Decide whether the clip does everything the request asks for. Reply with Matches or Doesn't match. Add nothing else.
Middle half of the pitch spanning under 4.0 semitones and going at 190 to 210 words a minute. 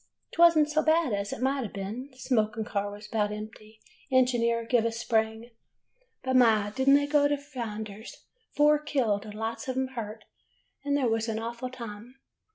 Matches